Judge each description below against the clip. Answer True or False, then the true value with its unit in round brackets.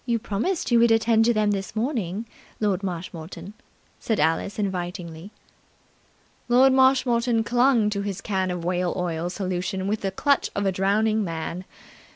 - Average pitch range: True (4.2 semitones)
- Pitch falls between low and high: False (200 Hz)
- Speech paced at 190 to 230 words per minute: False (155 wpm)